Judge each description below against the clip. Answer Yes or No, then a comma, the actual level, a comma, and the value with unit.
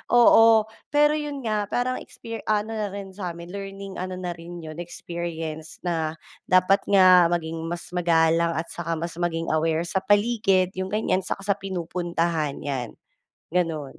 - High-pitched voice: No, medium, 175 Hz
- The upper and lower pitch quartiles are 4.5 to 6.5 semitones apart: No, average, 3.2 semitones